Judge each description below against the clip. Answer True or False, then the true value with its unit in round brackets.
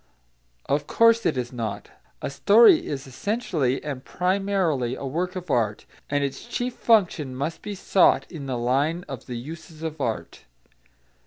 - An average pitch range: False (6.1 semitones)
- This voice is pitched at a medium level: True (150 Hz)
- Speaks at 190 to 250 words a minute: False (160 wpm)